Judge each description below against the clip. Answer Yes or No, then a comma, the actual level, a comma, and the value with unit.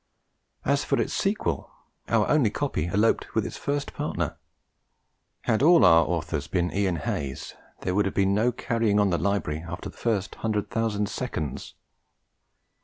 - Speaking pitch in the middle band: No, low, 100 Hz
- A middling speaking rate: Yes, average, 160 wpm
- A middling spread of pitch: Yes, average, 4.8 semitones